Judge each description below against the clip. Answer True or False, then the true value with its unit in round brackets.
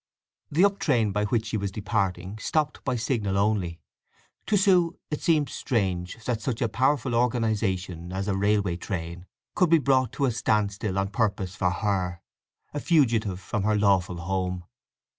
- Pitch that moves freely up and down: False (4.8 semitones)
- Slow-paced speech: False (165 wpm)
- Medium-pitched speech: False (105 Hz)